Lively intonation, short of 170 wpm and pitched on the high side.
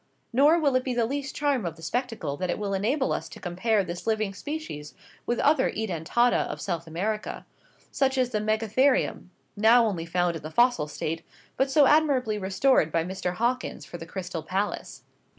No: wide, 6.4 semitones; average, 185 wpm; high, 215 Hz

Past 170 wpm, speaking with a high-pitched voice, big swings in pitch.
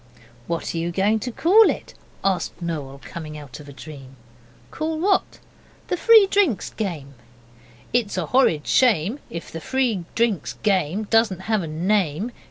No: average, 160 wpm; high, 195 Hz; wide, 7.1 semitones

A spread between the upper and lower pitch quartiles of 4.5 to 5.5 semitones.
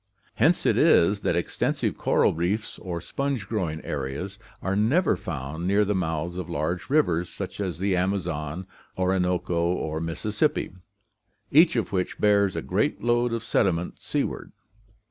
No: average, 3.7 semitones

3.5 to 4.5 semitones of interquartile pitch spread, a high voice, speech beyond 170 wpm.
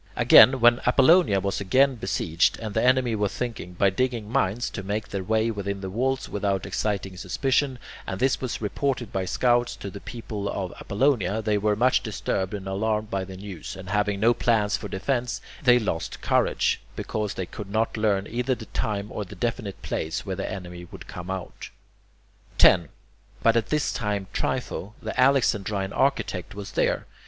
No: average, 3.8 semitones; low, 105 Hz; average, 180 wpm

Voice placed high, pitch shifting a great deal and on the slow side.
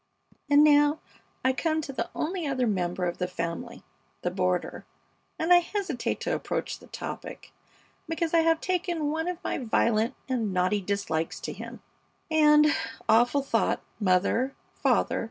No: very high, 265 Hz; wide, 7.8 semitones; average, 155 wpm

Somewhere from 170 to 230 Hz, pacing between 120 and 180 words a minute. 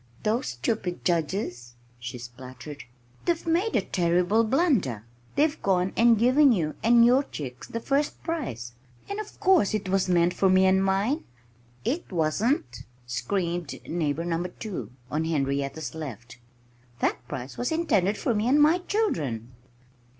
Yes: medium, 185 Hz; average, 145 wpm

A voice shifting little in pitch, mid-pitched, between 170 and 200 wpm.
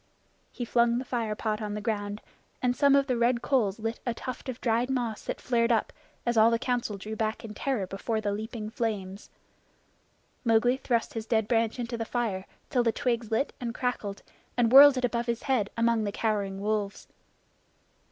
No: narrow, 2.3 semitones; high, 230 Hz; average, 195 wpm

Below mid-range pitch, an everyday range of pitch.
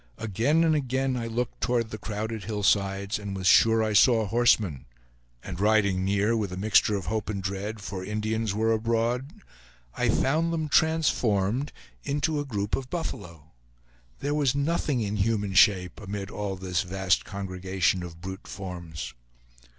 Yes: low, 105 Hz; average, 4.0 semitones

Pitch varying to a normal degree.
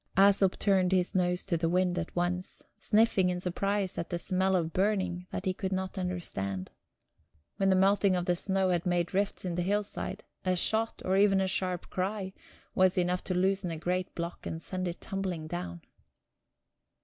No: narrow, 1.5 semitones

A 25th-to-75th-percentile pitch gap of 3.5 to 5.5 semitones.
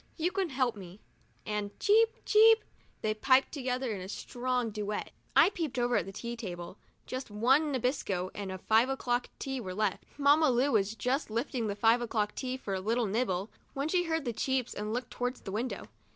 Yes: average, 4.2 semitones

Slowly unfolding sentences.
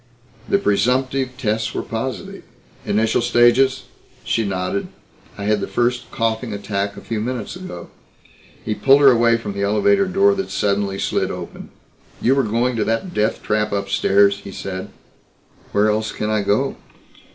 No: average, 160 wpm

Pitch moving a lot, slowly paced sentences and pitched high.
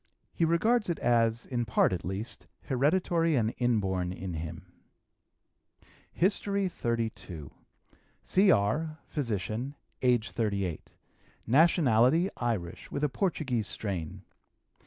No: wide, 8.1 semitones; slow, 100 wpm; low, 120 Hz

